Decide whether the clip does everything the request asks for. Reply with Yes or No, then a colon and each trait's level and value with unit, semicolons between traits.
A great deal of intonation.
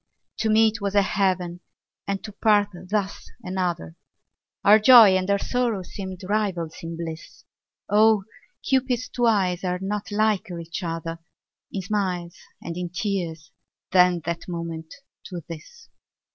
No: average, 3.5 semitones